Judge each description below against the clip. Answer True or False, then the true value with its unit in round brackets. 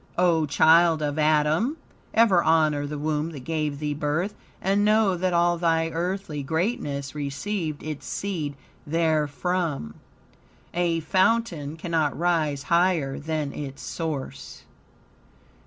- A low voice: False (160 Hz)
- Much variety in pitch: False (3.1 semitones)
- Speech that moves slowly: True (120 wpm)